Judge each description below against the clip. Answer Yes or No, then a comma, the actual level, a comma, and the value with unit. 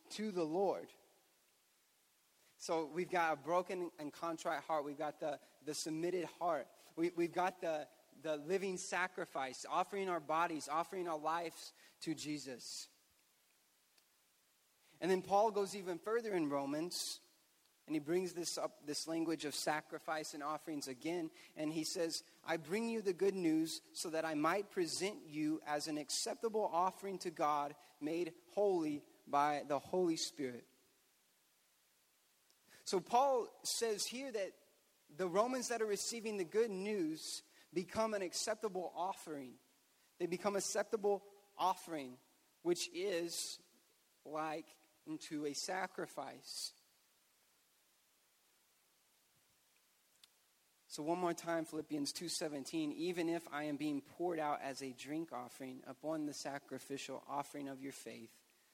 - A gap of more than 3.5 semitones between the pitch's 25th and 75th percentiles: Yes, average, 4.3 semitones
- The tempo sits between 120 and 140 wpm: Yes, slow, 135 wpm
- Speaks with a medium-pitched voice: Yes, medium, 170 Hz